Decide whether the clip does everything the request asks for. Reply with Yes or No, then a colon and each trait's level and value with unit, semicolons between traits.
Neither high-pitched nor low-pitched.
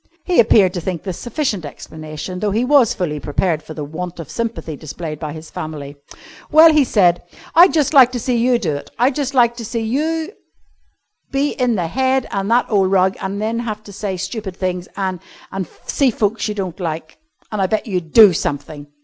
No: high, 200 Hz